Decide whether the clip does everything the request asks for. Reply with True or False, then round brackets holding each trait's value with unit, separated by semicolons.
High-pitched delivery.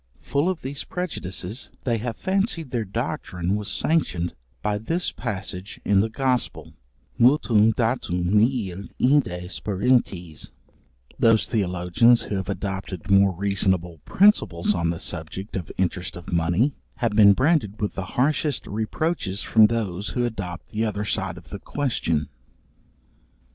False (105 Hz)